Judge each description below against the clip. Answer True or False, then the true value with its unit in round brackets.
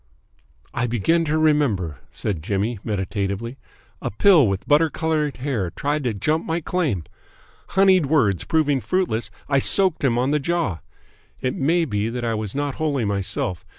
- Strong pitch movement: True (7.2 semitones)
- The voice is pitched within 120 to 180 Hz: True (135 Hz)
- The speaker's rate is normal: True (160 wpm)